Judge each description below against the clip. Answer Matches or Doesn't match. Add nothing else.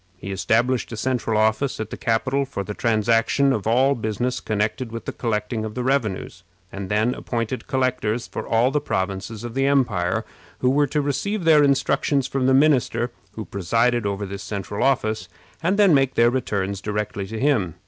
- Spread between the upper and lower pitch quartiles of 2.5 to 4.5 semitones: Matches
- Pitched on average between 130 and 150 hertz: Doesn't match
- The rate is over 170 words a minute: Matches